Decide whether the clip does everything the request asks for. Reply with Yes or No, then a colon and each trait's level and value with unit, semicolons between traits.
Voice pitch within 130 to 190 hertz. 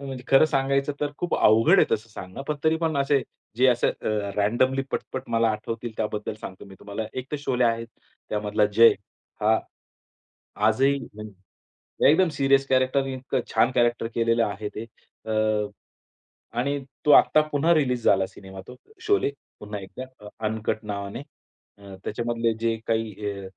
No: low, 115 Hz